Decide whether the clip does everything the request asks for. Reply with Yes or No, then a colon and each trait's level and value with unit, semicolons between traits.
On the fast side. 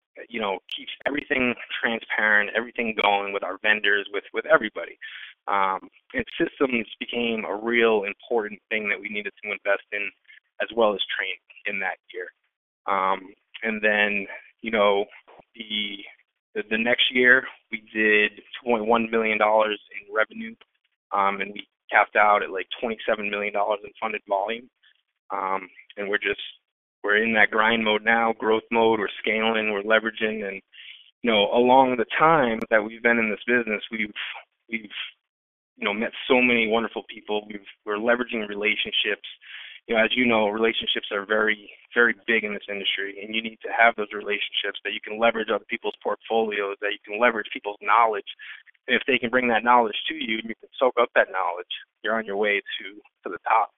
No: average, 180 wpm